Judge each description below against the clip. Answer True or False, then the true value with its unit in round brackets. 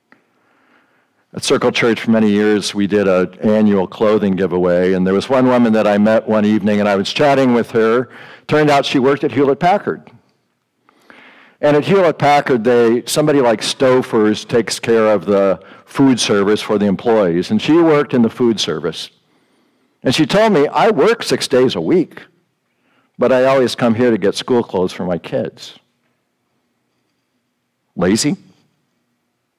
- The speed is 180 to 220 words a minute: False (165 wpm)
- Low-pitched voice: True (115 Hz)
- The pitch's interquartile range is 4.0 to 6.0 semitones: True (4.7 semitones)